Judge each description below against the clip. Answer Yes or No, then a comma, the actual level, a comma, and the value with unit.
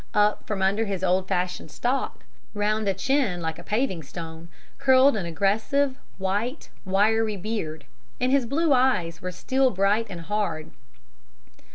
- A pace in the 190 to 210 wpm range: No, average, 150 wpm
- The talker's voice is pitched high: Yes, high, 205 Hz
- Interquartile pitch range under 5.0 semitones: No, wide, 5.4 semitones